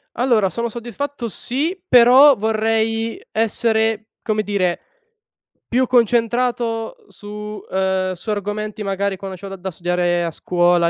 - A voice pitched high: Yes, high, 215 Hz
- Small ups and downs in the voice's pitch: No, average, 3.5 semitones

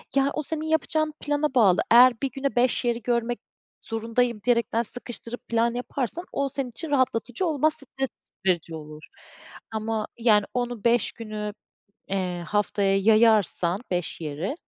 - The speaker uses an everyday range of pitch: Yes, average, 3.9 semitones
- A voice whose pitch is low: No, high, 235 Hz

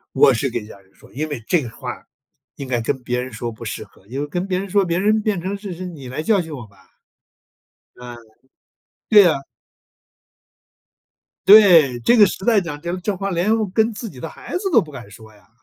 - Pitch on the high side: No, medium, 160 Hz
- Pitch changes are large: Yes, wide, 7.9 semitones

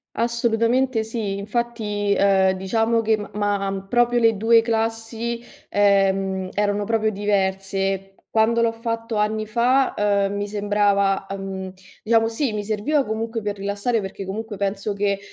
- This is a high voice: Yes, high, 210 Hz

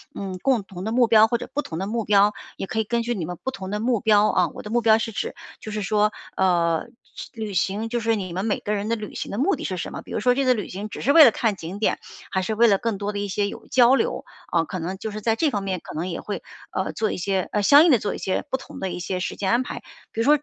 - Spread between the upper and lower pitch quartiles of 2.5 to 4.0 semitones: Yes, average, 3.4 semitones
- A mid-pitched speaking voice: No, high, 210 Hz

